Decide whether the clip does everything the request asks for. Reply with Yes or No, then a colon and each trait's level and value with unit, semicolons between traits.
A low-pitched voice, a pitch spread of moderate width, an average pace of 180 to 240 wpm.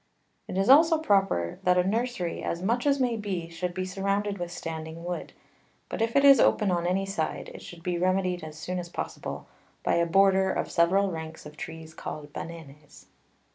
No: medium, 180 Hz; average, 3.1 semitones; average, 195 wpm